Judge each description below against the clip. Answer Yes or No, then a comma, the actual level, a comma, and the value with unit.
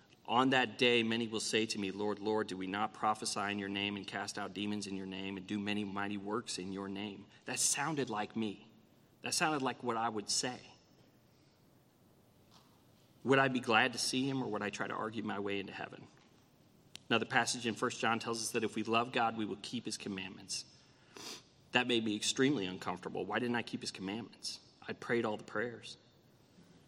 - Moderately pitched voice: No, low, 110 Hz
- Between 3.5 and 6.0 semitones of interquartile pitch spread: No, average, 3.1 semitones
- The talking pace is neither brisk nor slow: No, fast, 210 wpm